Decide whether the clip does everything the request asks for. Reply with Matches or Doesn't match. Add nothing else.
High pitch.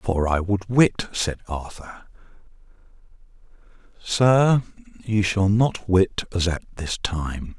Doesn't match